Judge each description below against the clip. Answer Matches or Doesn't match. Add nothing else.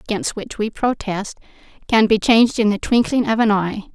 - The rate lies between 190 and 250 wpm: Matches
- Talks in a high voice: Matches